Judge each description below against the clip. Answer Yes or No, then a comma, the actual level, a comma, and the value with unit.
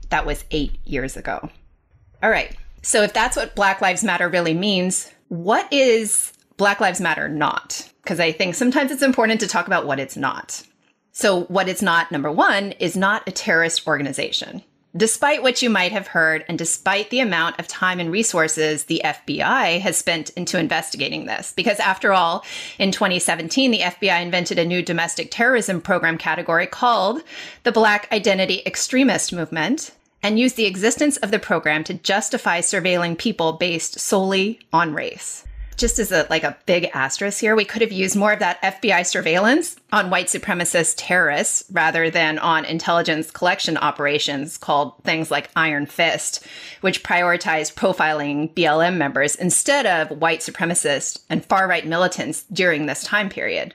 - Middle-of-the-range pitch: Yes, medium, 180 Hz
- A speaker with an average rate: Yes, average, 165 wpm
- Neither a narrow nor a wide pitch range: Yes, average, 4.3 semitones